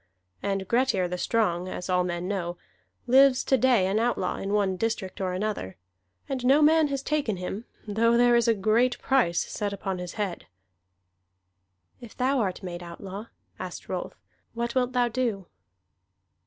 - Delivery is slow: No, average, 165 wpm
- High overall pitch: Yes, high, 215 Hz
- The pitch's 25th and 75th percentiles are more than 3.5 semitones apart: Yes, average, 4.8 semitones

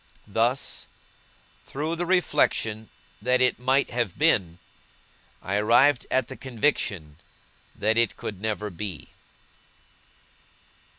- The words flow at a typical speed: No, slow, 105 wpm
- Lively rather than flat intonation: No, average, 4.1 semitones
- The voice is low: Yes, low, 115 Hz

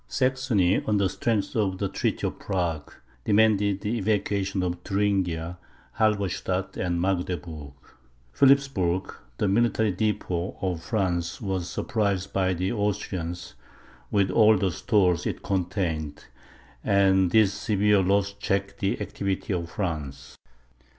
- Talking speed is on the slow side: Yes, slow, 125 wpm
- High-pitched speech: No, very low, 95 Hz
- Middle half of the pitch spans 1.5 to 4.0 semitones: Yes, narrow, 2.6 semitones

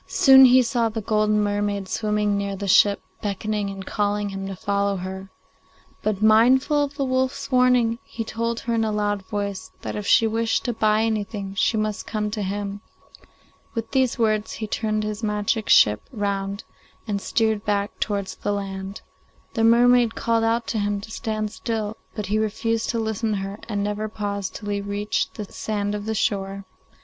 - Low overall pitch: No, high, 210 Hz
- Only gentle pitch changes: Yes, narrow, 1.9 semitones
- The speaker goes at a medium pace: Yes, average, 190 wpm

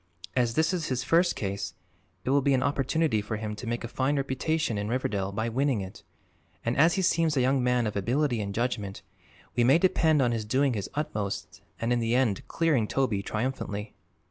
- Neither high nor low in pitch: No, low, 125 Hz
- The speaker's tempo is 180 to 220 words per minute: Yes, fast, 205 wpm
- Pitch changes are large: No, average, 4.8 semitones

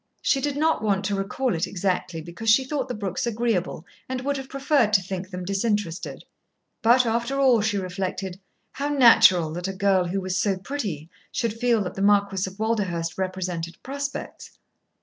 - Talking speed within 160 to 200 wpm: Yes, average, 180 wpm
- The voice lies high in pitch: Yes, high, 200 Hz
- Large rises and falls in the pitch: No, average, 4.8 semitones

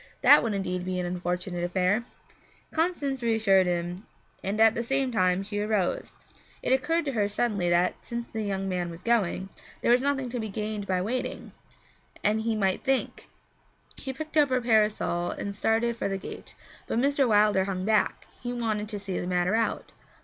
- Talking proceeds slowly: No, average, 185 wpm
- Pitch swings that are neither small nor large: Yes, average, 4.2 semitones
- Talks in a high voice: Yes, high, 210 Hz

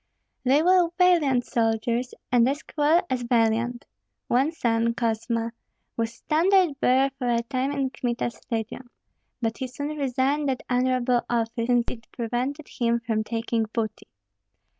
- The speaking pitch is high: Yes, high, 245 Hz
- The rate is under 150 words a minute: Yes, average, 140 wpm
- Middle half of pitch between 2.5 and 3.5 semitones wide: Yes, average, 2.9 semitones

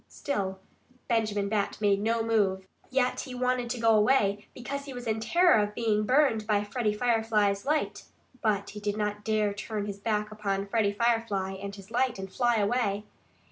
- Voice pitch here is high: Yes, high, 215 Hz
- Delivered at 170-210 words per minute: Yes, average, 180 wpm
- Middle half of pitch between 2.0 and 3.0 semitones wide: Yes, average, 2.7 semitones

